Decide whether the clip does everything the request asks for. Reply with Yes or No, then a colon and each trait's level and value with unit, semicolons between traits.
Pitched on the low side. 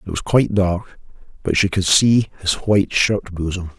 Yes: very low, 95 Hz